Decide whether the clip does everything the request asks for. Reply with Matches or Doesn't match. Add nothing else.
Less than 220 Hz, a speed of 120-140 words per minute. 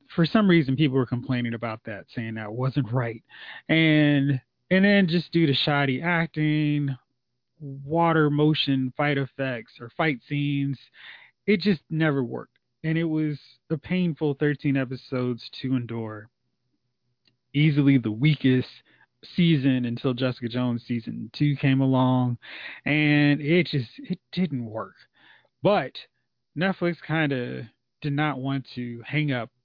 Matches